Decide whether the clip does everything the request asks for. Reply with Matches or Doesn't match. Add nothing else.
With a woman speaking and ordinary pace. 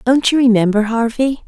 Matches